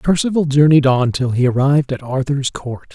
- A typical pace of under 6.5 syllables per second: Yes, 5.2 syllables/s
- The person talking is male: Yes, male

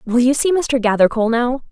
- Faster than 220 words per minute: No, fast, 210 wpm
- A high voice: Yes, very high, 250 Hz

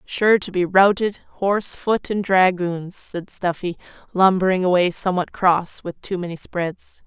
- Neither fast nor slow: Yes, average, 155 wpm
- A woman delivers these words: Yes, female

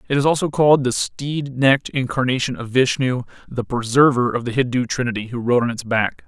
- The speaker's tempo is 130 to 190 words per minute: No, average, 200 wpm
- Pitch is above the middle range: No, low, 125 Hz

